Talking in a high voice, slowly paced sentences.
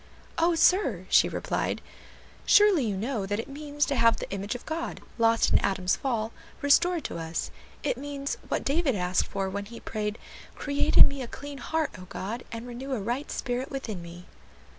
No: high, 245 Hz; average, 190 wpm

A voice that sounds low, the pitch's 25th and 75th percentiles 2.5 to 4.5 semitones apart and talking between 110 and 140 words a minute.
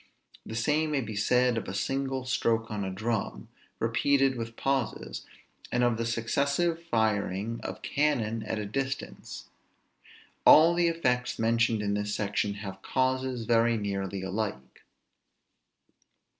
Yes: low, 115 Hz; average, 4.1 semitones; slow, 135 wpm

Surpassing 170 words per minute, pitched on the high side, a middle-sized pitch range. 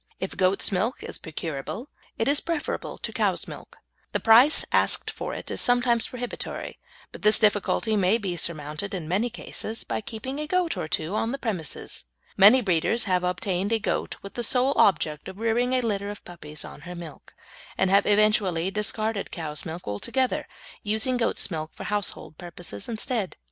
Yes: average, 180 wpm; high, 205 Hz; average, 4.8 semitones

